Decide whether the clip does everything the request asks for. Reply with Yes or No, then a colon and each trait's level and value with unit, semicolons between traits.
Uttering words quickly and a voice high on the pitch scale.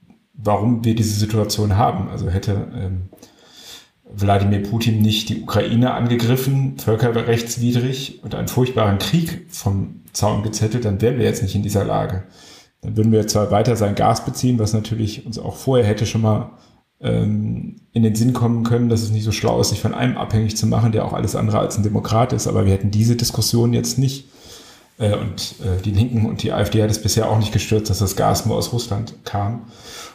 No: fast, 200 wpm; low, 110 Hz